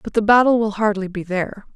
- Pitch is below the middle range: No, high, 210 Hz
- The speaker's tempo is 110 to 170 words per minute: No, fast, 240 wpm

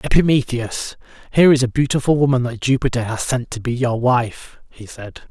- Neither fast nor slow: Yes, average, 180 wpm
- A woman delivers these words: No, male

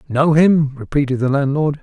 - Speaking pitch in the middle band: Yes, medium, 145 Hz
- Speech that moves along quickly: No, average, 165 wpm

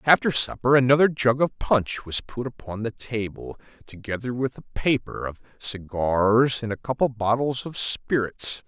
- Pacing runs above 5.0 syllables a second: No, 4.6 syllables/s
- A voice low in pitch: Yes, low, 120 Hz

